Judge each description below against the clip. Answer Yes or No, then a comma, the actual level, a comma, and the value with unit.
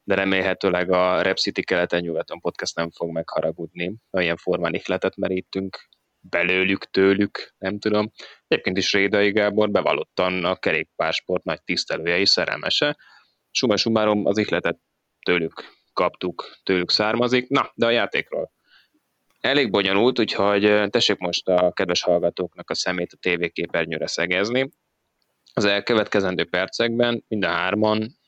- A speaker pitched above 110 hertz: No, very low, 95 Hz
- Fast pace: No, average, 130 wpm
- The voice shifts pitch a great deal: No, average, 2.8 semitones